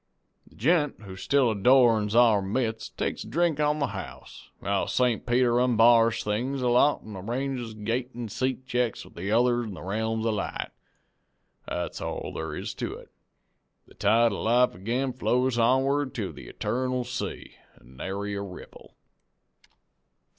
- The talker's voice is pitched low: Yes, low, 120 Hz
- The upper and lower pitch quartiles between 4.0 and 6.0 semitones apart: No, average, 3.3 semitones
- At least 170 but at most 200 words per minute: No, average, 160 wpm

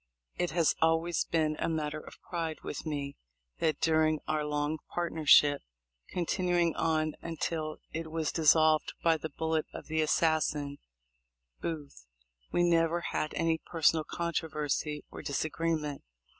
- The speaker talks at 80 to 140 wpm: Yes, slow, 135 wpm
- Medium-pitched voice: Yes, medium, 160 Hz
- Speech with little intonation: Yes, narrow, 1.4 semitones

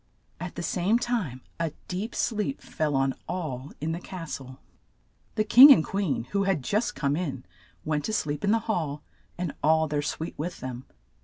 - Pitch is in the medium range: Yes, medium, 165 Hz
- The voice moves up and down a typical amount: No, wide, 5.8 semitones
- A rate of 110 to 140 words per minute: No, average, 185 wpm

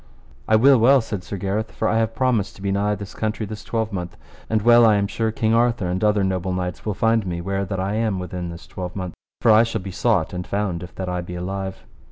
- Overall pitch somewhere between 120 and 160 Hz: No, low, 100 Hz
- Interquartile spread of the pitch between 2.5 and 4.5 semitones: Yes, average, 3.4 semitones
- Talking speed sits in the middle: No, fast, 250 wpm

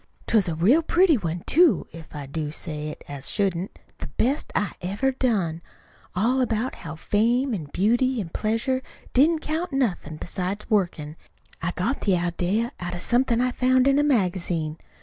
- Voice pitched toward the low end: No, high, 205 Hz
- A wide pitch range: Yes, wide, 7.1 semitones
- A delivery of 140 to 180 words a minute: Yes, average, 175 wpm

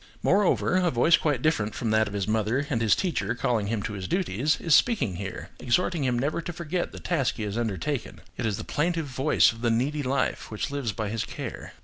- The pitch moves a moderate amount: No, wide, 6.0 semitones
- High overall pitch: No, low, 125 Hz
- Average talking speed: No, fast, 230 wpm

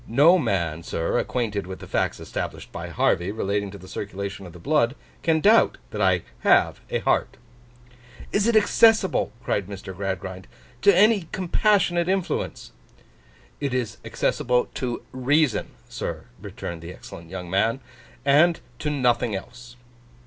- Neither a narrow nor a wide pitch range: No, wide, 8.8 semitones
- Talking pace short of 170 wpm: Yes, average, 145 wpm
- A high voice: No, low, 120 Hz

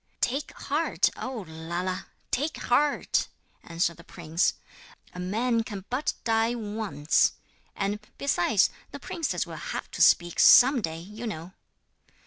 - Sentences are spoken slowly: Yes, slow, 130 wpm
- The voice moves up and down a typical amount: No, wide, 6.2 semitones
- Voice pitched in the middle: No, high, 210 Hz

